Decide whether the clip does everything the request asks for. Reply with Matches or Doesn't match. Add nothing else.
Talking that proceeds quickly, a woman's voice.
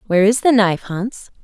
Matches